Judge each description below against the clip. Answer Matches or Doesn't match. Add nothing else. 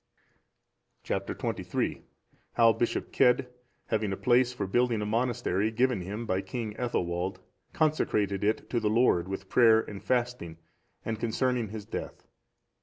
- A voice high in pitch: Doesn't match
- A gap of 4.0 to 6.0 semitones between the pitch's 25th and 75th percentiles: Doesn't match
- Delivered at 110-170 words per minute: Matches